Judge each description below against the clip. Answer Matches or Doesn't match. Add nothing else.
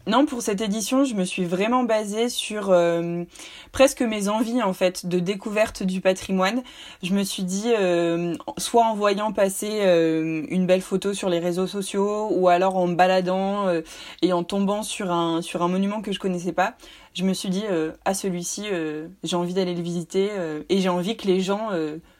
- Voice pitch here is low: Doesn't match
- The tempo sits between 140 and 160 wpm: Doesn't match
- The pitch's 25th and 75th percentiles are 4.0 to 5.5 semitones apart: Doesn't match